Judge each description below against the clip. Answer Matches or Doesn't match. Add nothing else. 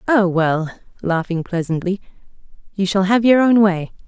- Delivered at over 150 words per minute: Doesn't match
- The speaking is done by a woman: Matches